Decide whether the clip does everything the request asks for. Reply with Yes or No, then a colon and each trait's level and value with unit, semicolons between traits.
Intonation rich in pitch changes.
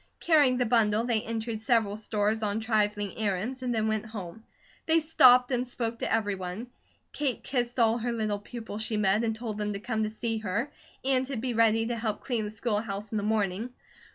No: narrow, 2.4 semitones